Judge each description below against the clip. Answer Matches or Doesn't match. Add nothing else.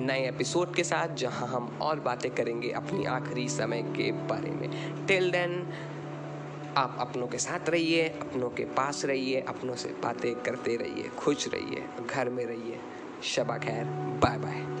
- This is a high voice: Doesn't match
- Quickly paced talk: Doesn't match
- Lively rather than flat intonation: Matches